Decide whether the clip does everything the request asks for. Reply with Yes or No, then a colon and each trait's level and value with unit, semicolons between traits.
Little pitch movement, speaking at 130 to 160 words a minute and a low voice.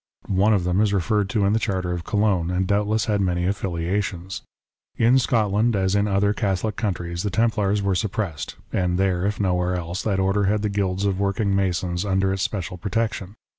No: narrow, 2.3 semitones; average, 195 wpm; low, 100 Hz